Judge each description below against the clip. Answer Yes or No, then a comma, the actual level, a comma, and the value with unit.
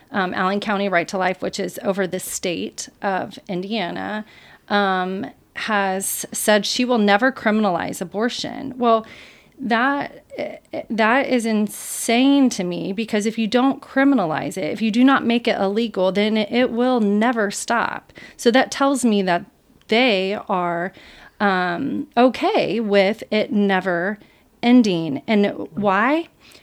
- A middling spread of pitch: Yes, average, 4.3 semitones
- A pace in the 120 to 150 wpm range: Yes, slow, 135 wpm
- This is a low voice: No, high, 220 Hz